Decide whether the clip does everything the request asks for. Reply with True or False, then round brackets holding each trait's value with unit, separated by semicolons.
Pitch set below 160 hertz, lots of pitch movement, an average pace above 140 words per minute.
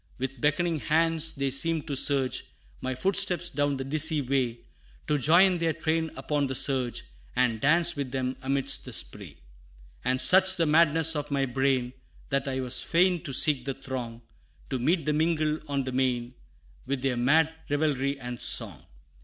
False (140 Hz; 3.6 semitones; 170 wpm)